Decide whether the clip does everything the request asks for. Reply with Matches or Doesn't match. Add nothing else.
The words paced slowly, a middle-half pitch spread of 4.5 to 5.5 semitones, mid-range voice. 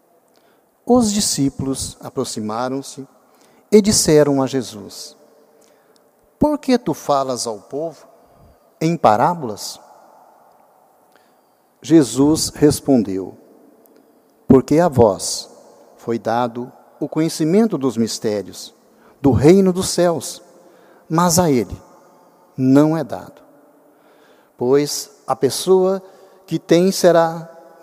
Matches